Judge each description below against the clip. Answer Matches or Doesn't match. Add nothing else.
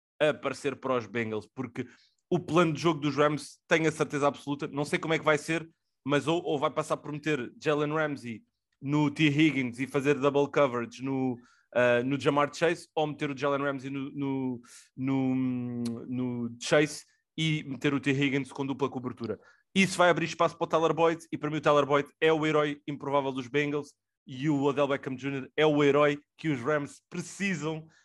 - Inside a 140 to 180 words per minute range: Doesn't match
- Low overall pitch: Doesn't match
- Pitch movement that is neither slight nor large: Doesn't match